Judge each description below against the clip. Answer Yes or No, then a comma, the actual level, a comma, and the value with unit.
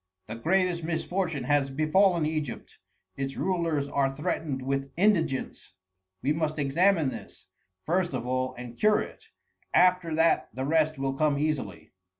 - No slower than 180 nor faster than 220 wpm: No, average, 145 wpm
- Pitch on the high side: No, medium, 155 Hz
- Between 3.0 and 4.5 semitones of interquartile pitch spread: Yes, average, 3.9 semitones